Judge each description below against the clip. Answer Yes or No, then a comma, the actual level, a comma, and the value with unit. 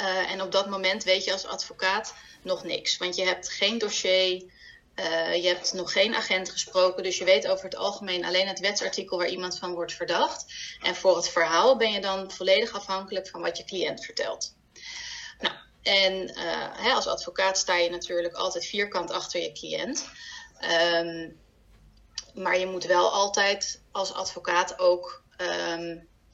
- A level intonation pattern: Yes, narrow, 1.5 semitones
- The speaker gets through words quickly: No, average, 170 wpm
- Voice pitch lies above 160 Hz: Yes, medium, 185 Hz